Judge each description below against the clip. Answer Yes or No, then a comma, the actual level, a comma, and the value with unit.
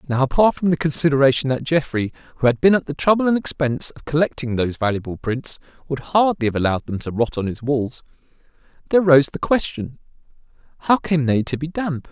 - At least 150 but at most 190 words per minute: No, average, 200 wpm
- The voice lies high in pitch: No, medium, 145 Hz